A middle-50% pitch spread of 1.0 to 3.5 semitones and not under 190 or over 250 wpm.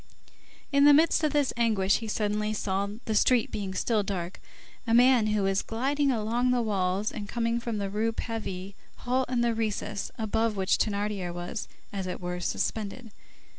No: average, 3.1 semitones; average, 175 wpm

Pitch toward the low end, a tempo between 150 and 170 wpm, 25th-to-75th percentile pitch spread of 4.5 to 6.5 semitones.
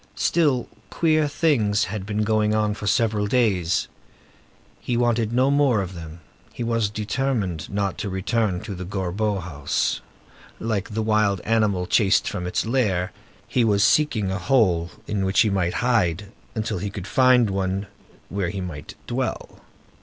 No: low, 105 Hz; average, 160 wpm; average, 3.5 semitones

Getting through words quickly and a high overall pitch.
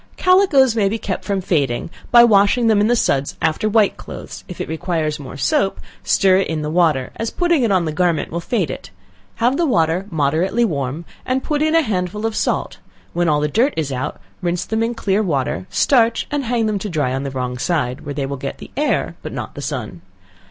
No: fast, 225 wpm; medium, 180 Hz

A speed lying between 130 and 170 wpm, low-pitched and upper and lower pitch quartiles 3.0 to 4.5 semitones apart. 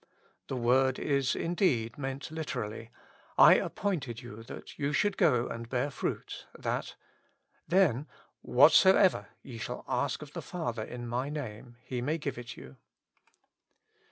Yes: average, 155 wpm; low, 130 Hz; average, 3.8 semitones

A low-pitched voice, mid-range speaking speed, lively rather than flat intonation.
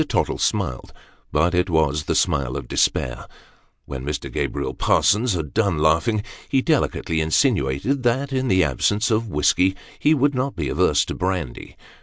Yes: very low, 90 Hz; average, 160 wpm; wide, 8.1 semitones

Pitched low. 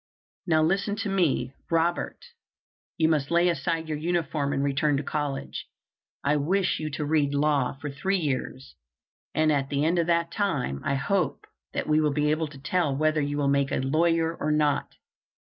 No: medium, 155 Hz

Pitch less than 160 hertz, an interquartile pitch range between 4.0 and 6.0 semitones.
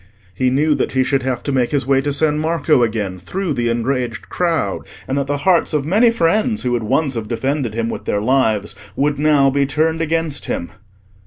Yes: medium, 140 Hz; average, 4.3 semitones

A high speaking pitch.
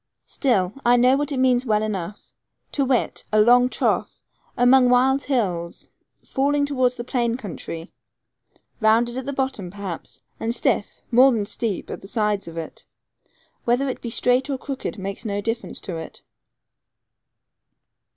Yes: high, 240 Hz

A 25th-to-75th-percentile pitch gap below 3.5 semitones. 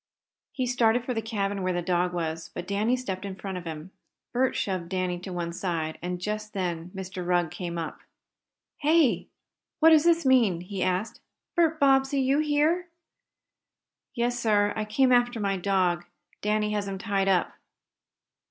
No: wide, 5.4 semitones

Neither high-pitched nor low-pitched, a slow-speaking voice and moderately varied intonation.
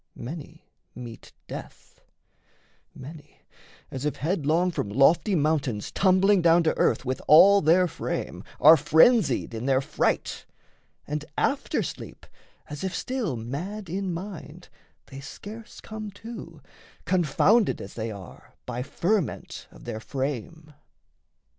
No: medium, 160 Hz; slow, 125 wpm; wide, 5.8 semitones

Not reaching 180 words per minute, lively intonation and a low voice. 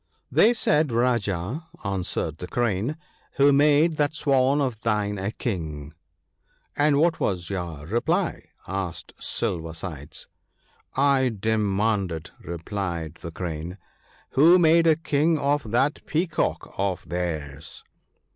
Yes: slow, 135 wpm; wide, 8.8 semitones; low, 105 Hz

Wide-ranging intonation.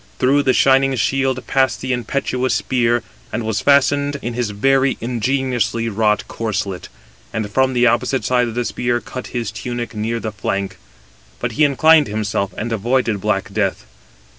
No: average, 3.4 semitones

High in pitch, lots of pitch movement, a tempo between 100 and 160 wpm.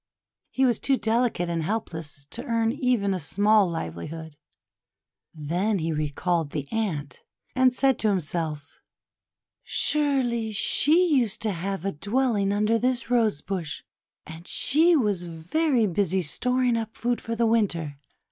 Yes: high, 205 Hz; wide, 6.6 semitones; average, 140 wpm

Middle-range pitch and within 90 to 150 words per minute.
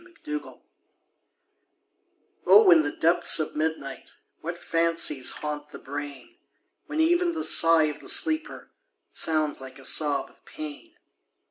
Yes: medium, 165 Hz; average, 140 wpm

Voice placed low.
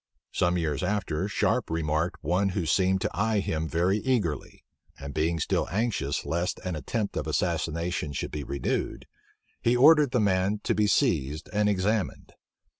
Yes: very low, 90 Hz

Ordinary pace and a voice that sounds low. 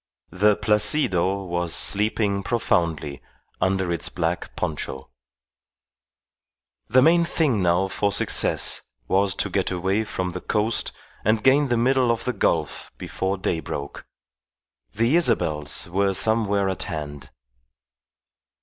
No: slow, 120 wpm; low, 100 Hz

